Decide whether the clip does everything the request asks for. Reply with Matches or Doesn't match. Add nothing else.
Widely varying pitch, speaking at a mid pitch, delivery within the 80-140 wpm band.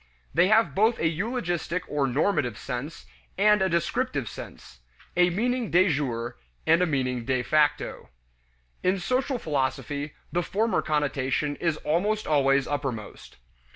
Matches